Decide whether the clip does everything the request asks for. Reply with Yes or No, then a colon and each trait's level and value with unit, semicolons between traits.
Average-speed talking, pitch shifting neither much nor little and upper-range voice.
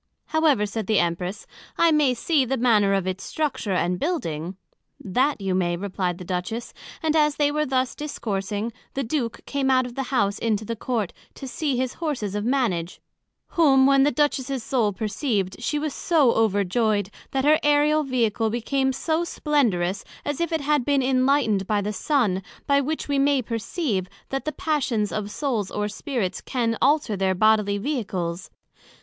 No: average, 175 wpm; wide, 5.9 semitones; high, 240 Hz